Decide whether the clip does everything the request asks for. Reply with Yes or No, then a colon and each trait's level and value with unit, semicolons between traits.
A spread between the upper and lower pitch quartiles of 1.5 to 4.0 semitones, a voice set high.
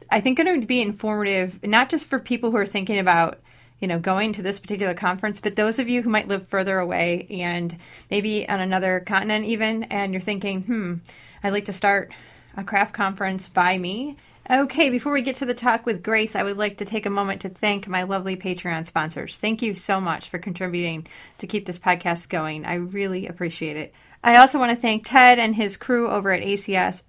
Yes: average, 3.2 semitones; high, 200 Hz